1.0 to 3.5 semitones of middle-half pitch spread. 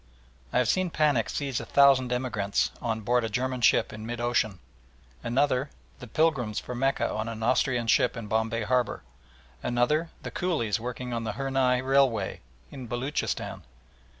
Yes: average, 2.9 semitones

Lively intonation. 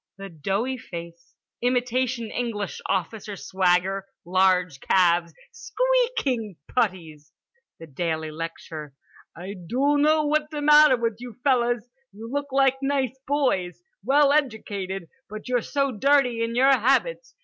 Yes: wide, 6.8 semitones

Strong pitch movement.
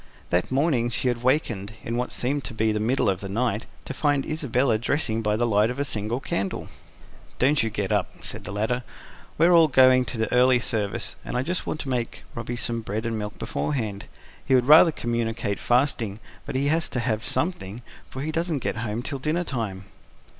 No: average, 3.9 semitones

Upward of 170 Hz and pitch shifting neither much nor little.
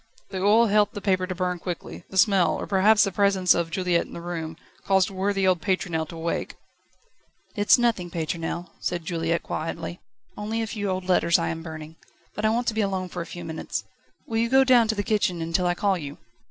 Yes: medium, 185 Hz; average, 3.4 semitones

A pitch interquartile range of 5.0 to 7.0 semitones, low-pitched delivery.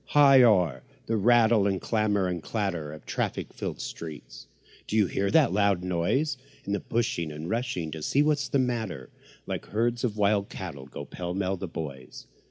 Yes: wide, 5.5 semitones; low, 100 Hz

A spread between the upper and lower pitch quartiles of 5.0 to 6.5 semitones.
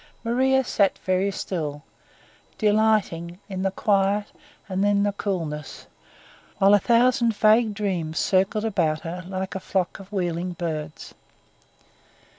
No: average, 3.5 semitones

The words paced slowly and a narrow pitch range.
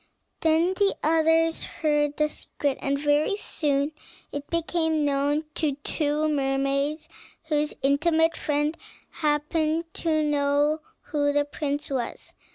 Yes: slow, 120 wpm; narrow, 1.8 semitones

